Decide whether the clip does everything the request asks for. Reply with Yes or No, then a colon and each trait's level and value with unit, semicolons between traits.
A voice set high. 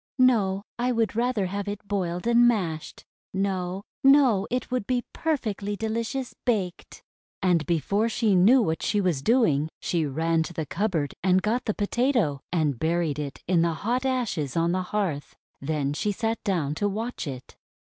Yes: high, 195 Hz